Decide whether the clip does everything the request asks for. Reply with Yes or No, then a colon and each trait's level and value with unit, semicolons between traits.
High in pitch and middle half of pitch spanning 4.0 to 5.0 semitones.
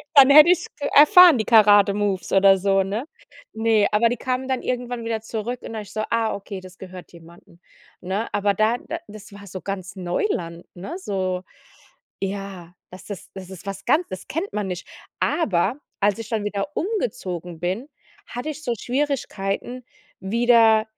Yes: high, 210 Hz; average, 4.3 semitones